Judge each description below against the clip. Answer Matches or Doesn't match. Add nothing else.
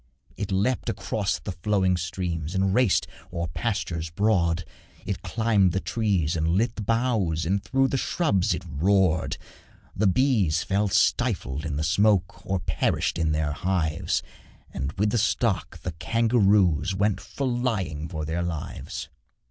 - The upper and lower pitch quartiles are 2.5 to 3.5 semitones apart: Doesn't match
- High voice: Doesn't match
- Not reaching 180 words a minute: Matches